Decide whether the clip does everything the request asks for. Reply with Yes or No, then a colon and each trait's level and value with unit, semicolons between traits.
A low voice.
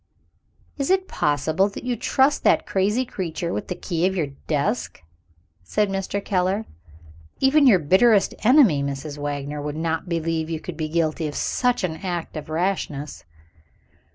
No: medium, 175 Hz